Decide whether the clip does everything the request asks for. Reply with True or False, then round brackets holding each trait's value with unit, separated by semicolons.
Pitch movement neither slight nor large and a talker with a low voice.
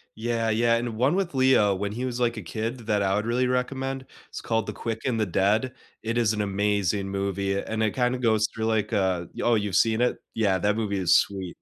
True (3.0 semitones; 110 Hz)